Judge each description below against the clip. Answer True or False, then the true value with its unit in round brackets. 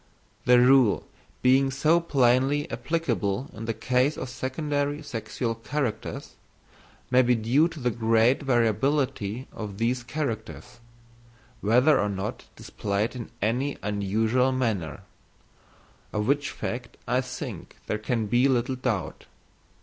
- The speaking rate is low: True (120 wpm)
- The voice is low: True (125 Hz)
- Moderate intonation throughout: True (3.4 semitones)